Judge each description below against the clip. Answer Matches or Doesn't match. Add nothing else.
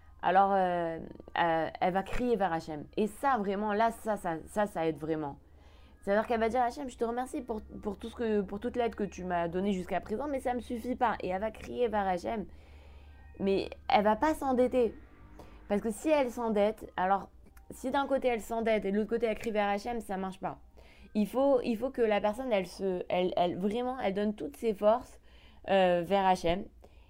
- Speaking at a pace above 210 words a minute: Matches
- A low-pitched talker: Doesn't match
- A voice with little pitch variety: Doesn't match